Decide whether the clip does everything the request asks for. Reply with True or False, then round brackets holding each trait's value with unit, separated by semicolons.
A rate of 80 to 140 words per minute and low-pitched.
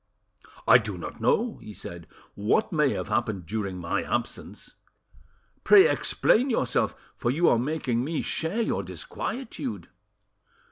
True (135 wpm; 130 Hz)